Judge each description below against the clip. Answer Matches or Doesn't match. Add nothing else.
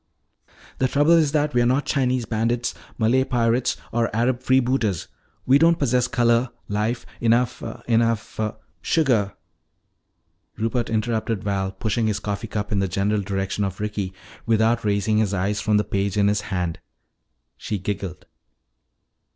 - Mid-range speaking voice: Doesn't match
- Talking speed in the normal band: Matches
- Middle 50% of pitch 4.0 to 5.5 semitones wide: Doesn't match